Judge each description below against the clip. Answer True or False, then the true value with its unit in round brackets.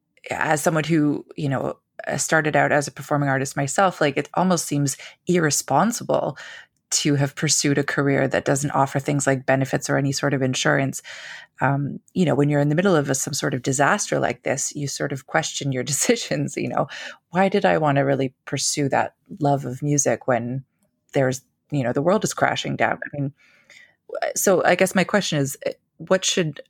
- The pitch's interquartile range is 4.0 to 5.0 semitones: False (2.8 semitones)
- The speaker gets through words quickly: False (195 wpm)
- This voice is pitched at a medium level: True (145 Hz)